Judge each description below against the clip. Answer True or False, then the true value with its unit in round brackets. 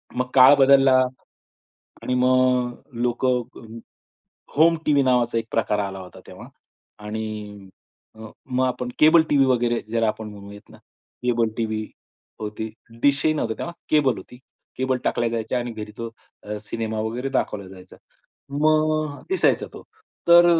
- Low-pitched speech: True (120 Hz)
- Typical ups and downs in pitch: True (3.6 semitones)